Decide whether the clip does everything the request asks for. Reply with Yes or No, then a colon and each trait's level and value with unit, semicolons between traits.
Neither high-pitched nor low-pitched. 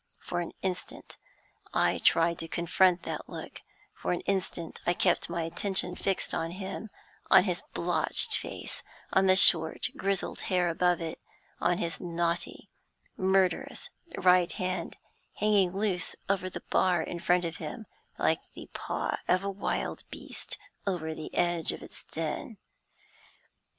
Yes: medium, 180 Hz